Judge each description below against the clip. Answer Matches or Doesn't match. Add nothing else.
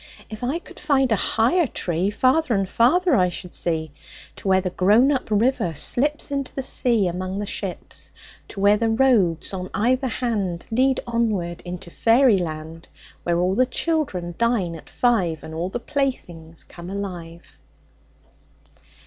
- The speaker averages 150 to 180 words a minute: Matches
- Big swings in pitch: Matches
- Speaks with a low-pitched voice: Doesn't match